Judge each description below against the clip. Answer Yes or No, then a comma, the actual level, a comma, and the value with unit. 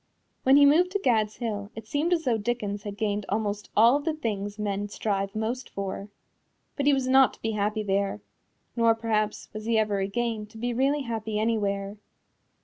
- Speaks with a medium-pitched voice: No, high, 220 Hz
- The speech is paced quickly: No, average, 195 wpm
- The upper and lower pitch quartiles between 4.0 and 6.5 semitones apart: No, average, 2.9 semitones